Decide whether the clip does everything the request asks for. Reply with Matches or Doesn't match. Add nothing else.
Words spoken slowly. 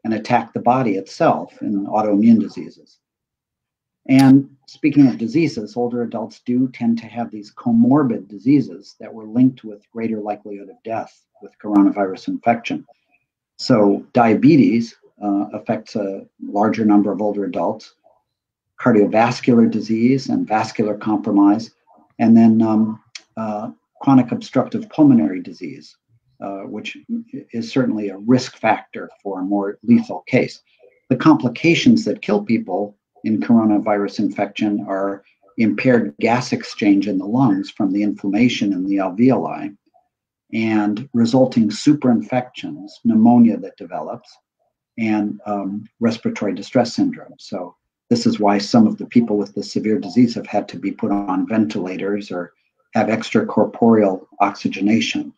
Matches